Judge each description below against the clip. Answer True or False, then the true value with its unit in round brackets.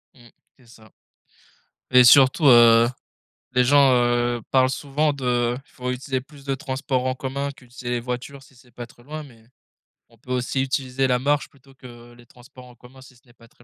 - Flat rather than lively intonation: True (1.8 semitones)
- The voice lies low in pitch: True (125 Hz)